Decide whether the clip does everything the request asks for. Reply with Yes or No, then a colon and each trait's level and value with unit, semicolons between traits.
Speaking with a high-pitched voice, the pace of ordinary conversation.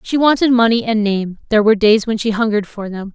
No: high, 220 Hz; fast, 250 wpm